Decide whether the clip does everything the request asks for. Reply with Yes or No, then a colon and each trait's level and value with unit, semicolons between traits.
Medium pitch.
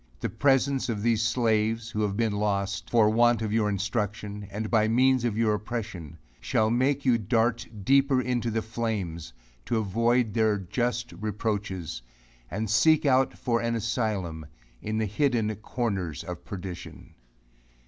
No: low, 110 Hz